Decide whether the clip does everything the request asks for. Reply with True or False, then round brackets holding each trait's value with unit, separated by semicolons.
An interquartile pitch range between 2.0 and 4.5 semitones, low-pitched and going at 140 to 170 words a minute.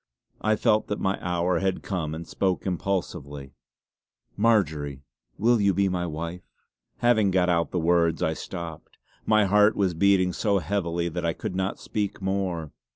True (2.9 semitones; 90 Hz; 160 wpm)